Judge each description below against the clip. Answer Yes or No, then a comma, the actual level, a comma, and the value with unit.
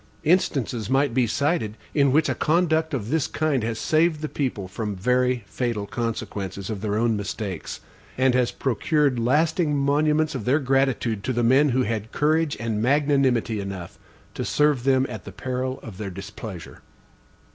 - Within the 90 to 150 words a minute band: No, average, 170 wpm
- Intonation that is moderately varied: Yes, average, 4.9 semitones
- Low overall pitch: Yes, low, 130 Hz